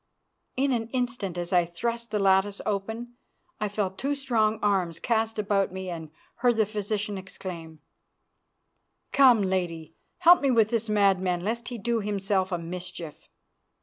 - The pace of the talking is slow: No, average, 150 wpm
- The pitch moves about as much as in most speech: Yes, average, 3.9 semitones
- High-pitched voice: Yes, high, 205 Hz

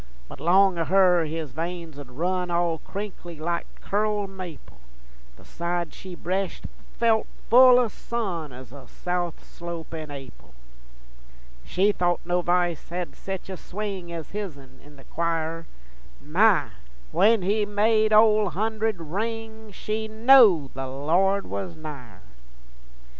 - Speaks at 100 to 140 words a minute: Yes, slow, 135 wpm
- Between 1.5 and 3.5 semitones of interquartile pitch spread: No, average, 4.3 semitones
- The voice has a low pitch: No, medium, 180 Hz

